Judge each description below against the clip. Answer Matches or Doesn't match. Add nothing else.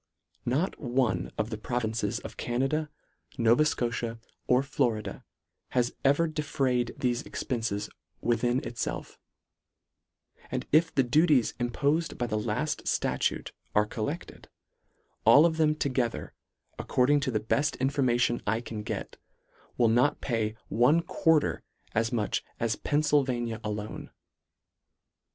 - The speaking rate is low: Matches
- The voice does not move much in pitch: Doesn't match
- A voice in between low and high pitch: Doesn't match